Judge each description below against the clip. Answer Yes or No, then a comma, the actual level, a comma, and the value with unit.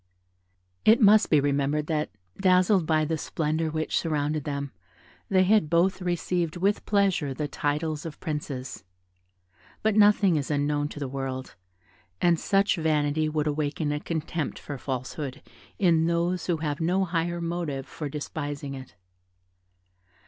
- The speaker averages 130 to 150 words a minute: Yes, average, 140 wpm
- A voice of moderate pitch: Yes, medium, 155 Hz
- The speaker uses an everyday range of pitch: Yes, average, 3.1 semitones